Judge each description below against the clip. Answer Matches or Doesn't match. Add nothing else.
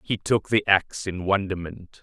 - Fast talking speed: Doesn't match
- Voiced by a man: Matches